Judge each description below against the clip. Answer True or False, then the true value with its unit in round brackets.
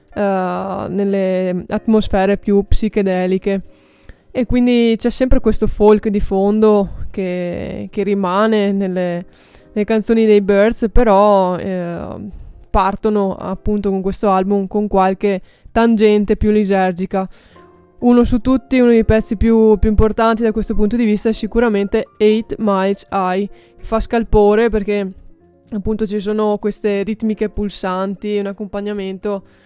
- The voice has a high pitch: True (210 Hz)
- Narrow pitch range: True (2.1 semitones)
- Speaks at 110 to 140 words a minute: True (125 wpm)